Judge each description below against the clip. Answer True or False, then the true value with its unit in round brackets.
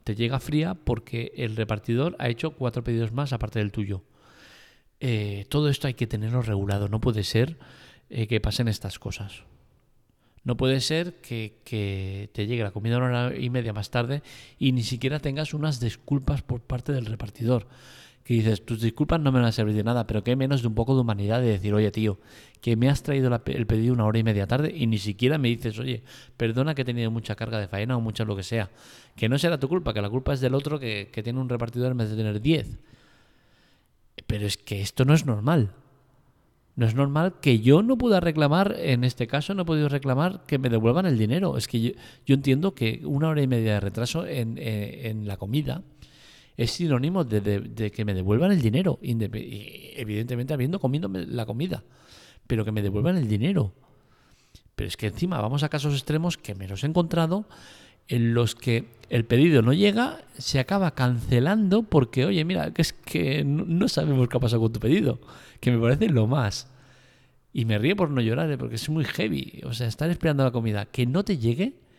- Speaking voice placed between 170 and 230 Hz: False (125 Hz)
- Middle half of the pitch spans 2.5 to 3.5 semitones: False (4.3 semitones)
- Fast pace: True (215 wpm)